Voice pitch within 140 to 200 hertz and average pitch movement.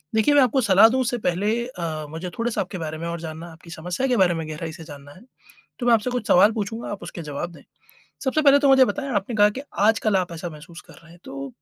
No: medium, 185 Hz; wide, 6.2 semitones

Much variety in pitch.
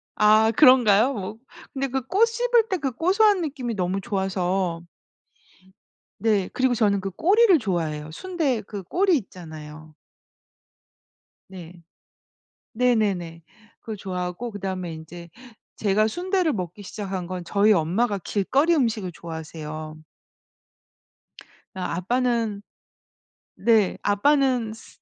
Yes: wide, 6.2 semitones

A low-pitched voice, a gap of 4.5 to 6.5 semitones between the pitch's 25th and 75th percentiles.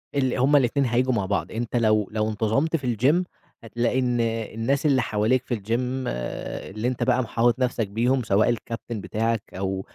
No: low, 120 Hz; average, 2.9 semitones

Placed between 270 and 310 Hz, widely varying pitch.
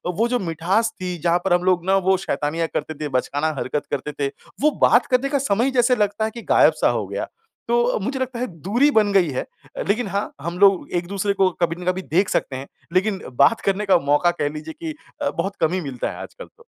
No: high, 190 Hz; wide, 5.7 semitones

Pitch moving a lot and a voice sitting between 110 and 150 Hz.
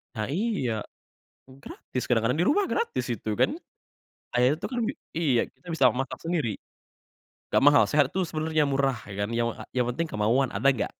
Yes: wide, 5.8 semitones; low, 135 Hz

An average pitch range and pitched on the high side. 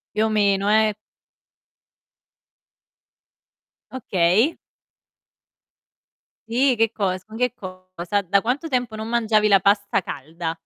Yes: average, 3.4 semitones; high, 210 Hz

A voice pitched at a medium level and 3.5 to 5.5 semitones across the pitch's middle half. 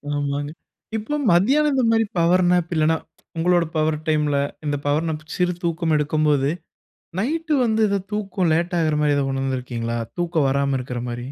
Yes: medium, 160 Hz; average, 4.0 semitones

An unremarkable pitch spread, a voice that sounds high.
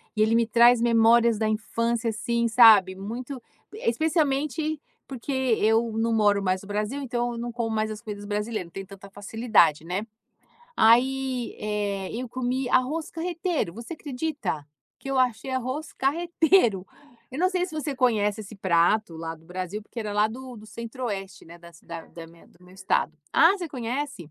Yes: average, 4.2 semitones; high, 230 Hz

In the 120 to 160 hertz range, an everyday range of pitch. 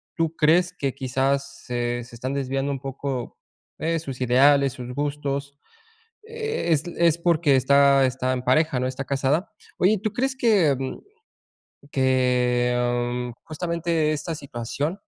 Yes: medium, 140 Hz; average, 3.9 semitones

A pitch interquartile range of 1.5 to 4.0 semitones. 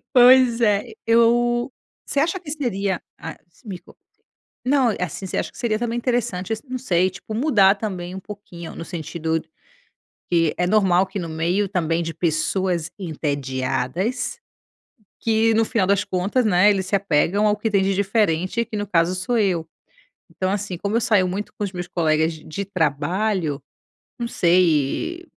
No: average, 4.7 semitones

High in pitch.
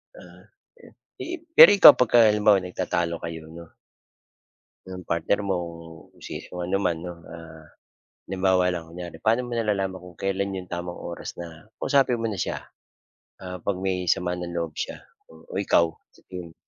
No: very low, 90 Hz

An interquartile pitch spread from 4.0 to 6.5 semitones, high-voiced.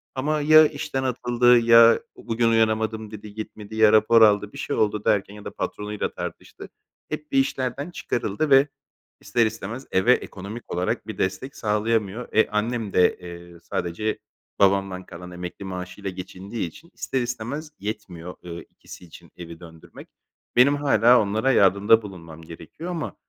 No: average, 4.3 semitones; low, 110 Hz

